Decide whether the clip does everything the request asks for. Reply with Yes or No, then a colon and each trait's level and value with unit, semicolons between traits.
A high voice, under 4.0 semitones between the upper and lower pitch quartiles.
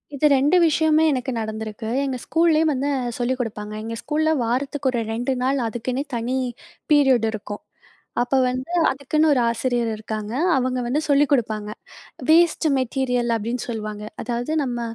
Yes: very high, 255 Hz; average, 3.6 semitones